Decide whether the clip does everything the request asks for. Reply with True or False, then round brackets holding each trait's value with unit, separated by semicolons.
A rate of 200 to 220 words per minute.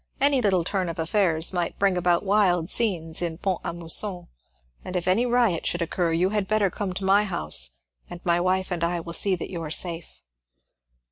True (205 wpm)